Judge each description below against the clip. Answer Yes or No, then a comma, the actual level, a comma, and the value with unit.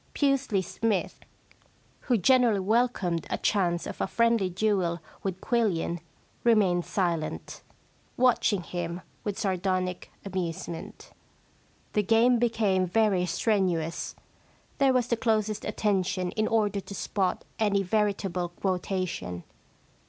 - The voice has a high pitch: Yes, high, 195 Hz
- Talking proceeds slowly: Yes, slow, 110 wpm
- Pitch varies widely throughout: No, average, 3.6 semitones